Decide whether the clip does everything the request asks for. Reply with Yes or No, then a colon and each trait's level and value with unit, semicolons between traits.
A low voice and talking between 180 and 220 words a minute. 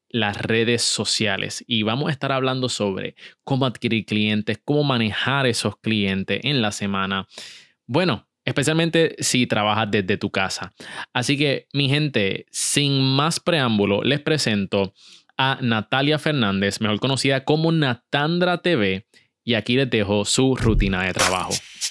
No: low, 120 Hz; average, 140 wpm